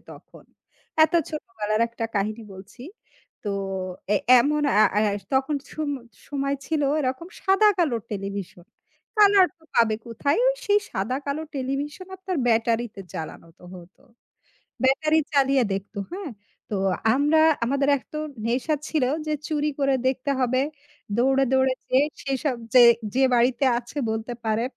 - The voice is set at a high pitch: Yes, very high, 265 Hz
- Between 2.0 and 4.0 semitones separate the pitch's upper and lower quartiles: No, average, 4.4 semitones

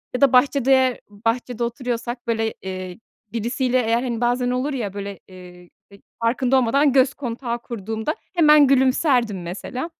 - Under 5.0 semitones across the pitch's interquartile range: Yes, average, 2.9 semitones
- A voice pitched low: No, high, 240 Hz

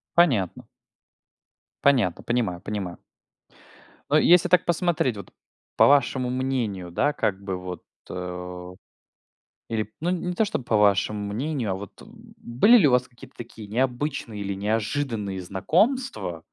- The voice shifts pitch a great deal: Yes, wide, 6.9 semitones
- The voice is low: Yes, low, 115 Hz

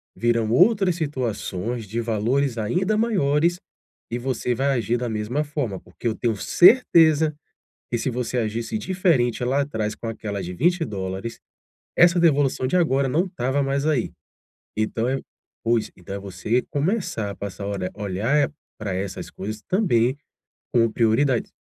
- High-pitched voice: No, low, 120 Hz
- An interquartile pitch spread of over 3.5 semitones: Yes, average, 5.3 semitones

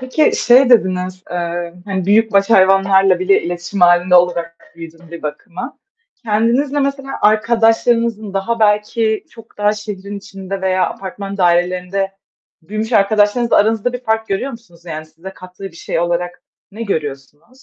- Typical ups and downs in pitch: Yes, average, 4.0 semitones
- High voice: Yes, high, 195 Hz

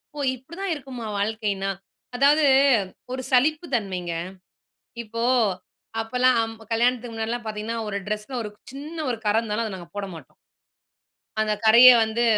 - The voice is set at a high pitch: Yes, high, 230 Hz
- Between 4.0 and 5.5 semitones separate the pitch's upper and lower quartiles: No, average, 3.2 semitones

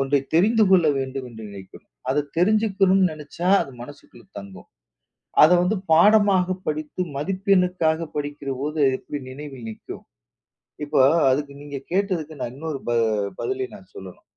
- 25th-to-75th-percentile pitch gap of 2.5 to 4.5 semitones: No, average, 5.1 semitones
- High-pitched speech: No, medium, 155 Hz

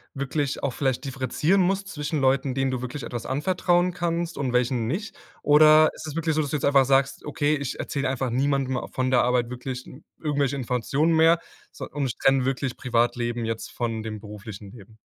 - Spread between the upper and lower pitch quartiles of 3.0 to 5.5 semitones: Yes, average, 3.4 semitones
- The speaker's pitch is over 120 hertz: Yes, low, 135 Hz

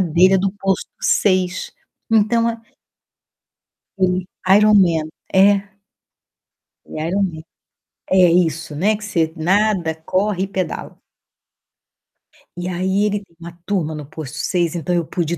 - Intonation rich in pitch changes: No, average, 3.0 semitones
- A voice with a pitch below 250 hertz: Yes, medium, 185 Hz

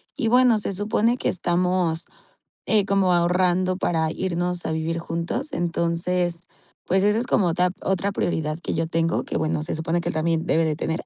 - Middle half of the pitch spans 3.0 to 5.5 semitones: No, narrow, 2.6 semitones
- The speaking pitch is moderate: Yes, medium, 175 Hz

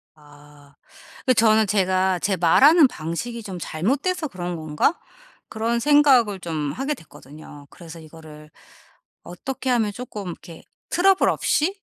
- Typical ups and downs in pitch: No, wide, 7.8 semitones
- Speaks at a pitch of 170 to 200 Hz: Yes, high, 190 Hz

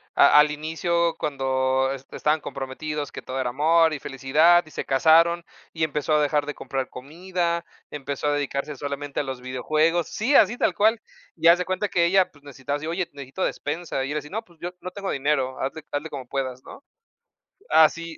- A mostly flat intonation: No, average, 3.7 semitones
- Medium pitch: Yes, medium, 150 Hz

